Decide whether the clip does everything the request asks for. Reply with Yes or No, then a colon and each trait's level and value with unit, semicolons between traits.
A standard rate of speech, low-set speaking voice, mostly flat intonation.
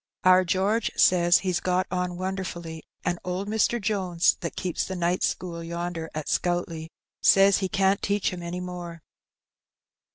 No: average, 155 wpm; medium, 180 Hz; narrow, 1.7 semitones